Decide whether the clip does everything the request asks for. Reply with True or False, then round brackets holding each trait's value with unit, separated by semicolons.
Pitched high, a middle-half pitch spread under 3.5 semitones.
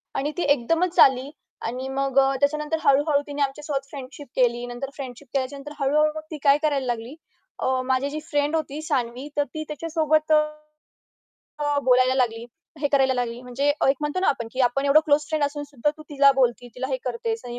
True (275 Hz; 2.8 semitones)